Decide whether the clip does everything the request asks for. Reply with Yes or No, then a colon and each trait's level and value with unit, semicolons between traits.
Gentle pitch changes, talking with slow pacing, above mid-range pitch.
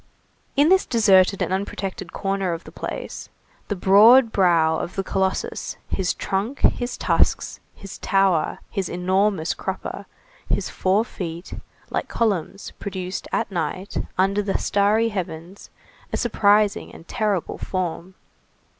Yes: narrow, 2.2 semitones; slow, 130 wpm; high, 195 Hz